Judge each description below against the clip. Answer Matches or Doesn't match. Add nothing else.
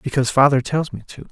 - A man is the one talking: Matches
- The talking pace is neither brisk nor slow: Doesn't match